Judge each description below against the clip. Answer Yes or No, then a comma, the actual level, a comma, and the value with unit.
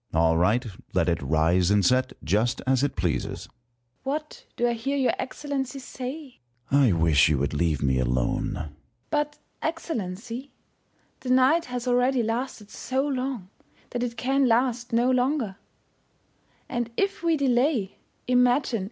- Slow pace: No, average, 160 wpm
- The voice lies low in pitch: No, high, 235 Hz